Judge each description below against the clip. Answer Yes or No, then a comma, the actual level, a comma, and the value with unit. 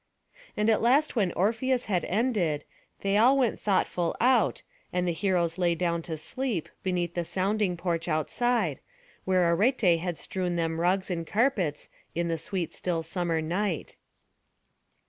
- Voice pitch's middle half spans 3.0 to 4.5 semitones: Yes, average, 3.9 semitones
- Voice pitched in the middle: Yes, medium, 180 Hz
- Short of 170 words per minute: Yes, average, 150 wpm